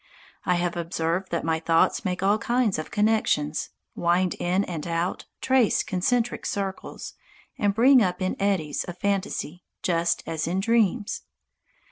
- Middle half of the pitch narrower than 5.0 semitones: Yes, average, 3.4 semitones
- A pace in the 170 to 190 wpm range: No, average, 145 wpm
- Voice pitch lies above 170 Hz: Yes, medium, 185 Hz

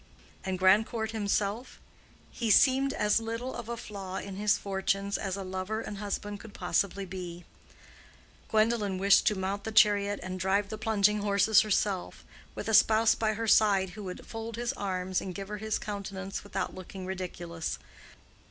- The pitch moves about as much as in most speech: No, narrow, 2.3 semitones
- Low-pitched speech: No, high, 200 Hz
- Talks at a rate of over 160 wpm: Yes, average, 170 wpm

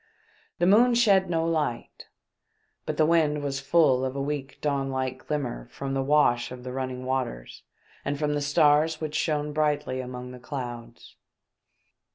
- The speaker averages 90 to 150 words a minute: No, average, 165 wpm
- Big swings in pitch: No, average, 2.9 semitones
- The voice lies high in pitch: No, medium, 140 Hz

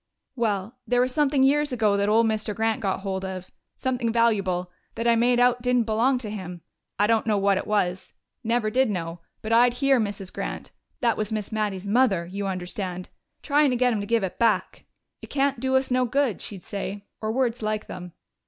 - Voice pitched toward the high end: Yes, high, 220 Hz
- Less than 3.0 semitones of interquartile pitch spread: No, average, 3.7 semitones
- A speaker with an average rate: No, fast, 210 wpm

